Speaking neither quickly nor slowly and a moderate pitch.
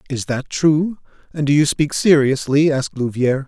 Yes: average, 175 wpm; medium, 145 Hz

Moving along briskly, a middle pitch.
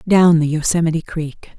No: average, 150 wpm; medium, 160 Hz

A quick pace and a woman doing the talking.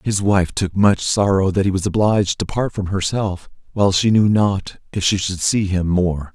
No: fast, 215 wpm; male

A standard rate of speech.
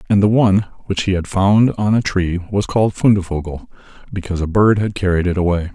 No: fast, 210 wpm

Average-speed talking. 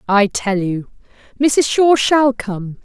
Yes: average, 150 wpm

